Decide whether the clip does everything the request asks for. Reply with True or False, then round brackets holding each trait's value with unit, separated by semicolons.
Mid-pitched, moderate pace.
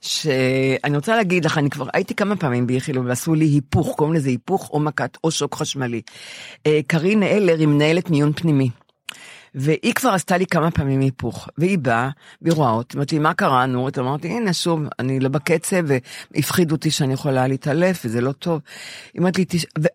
False (150 Hz; 175 wpm)